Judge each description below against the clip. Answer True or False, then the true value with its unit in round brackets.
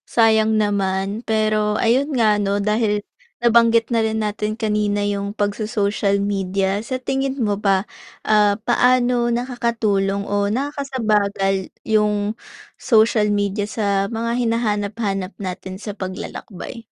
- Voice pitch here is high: True (210 Hz)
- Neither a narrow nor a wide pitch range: False (2.2 semitones)